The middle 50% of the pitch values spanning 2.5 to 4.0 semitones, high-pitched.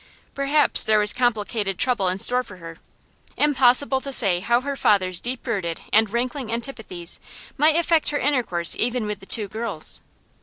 No: average, 5.2 semitones; high, 235 Hz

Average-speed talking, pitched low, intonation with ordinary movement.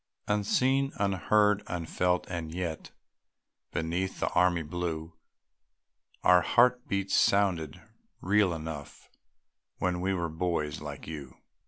No: slow, 110 wpm; very low, 90 Hz; average, 3.5 semitones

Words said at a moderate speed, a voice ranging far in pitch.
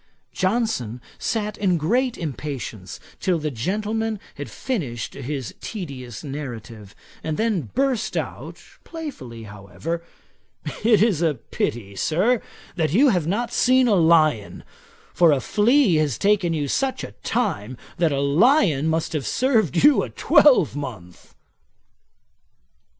No: slow, 130 wpm; wide, 8.8 semitones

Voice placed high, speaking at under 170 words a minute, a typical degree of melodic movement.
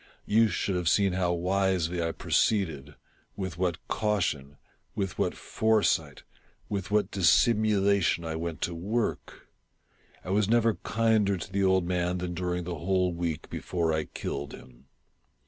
No: very low, 90 Hz; average, 160 wpm; average, 3.0 semitones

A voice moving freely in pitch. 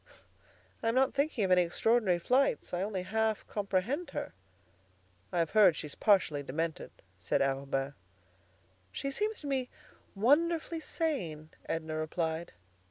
Yes: wide, 8.4 semitones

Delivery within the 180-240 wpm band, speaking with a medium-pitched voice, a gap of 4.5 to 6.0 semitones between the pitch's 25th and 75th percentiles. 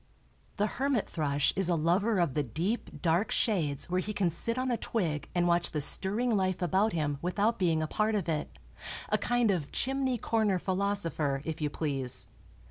Yes: average, 185 wpm; medium, 180 Hz; wide, 5.4 semitones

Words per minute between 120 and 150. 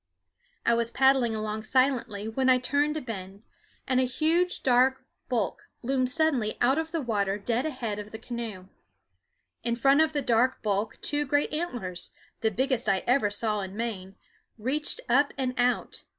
No: average, 170 wpm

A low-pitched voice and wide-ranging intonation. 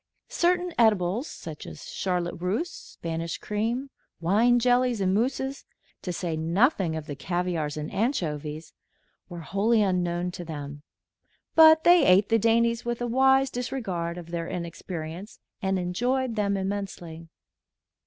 No: high, 190 Hz; wide, 6.0 semitones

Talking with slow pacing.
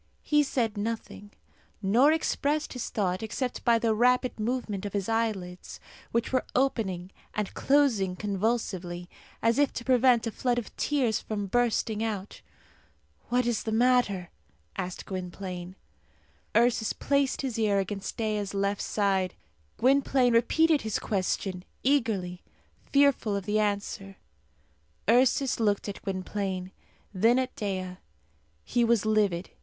Yes: slow, 130 wpm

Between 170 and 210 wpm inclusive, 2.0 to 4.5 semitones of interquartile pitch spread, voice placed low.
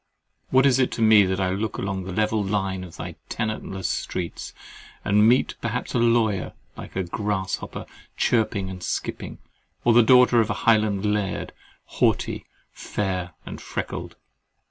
No: average, 155 wpm; average, 3.1 semitones; low, 105 Hz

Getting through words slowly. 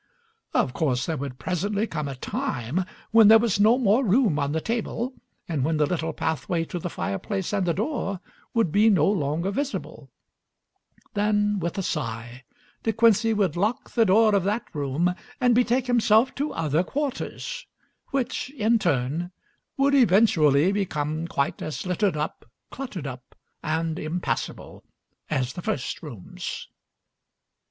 No: average, 150 wpm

